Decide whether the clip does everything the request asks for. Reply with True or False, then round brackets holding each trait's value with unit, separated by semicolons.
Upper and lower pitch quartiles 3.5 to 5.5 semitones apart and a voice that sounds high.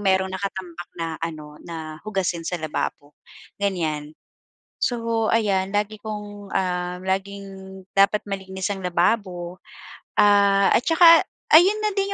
False (3.0 semitones; 195 Hz)